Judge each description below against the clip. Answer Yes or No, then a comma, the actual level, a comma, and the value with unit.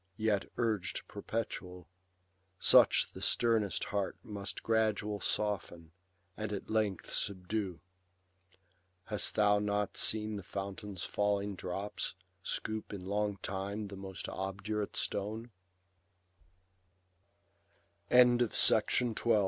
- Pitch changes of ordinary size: No, narrow, 1.7 semitones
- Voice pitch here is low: Yes, low, 100 Hz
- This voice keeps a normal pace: No, slow, 90 wpm